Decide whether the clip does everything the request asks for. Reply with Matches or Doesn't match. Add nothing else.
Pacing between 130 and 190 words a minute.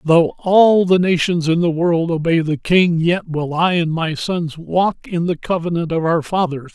Doesn't match